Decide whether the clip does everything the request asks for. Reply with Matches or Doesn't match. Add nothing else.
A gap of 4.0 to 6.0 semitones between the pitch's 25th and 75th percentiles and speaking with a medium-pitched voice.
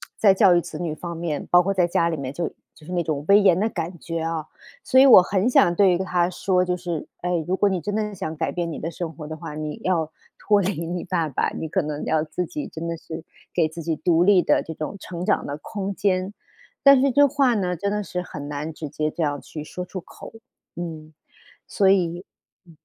Doesn't match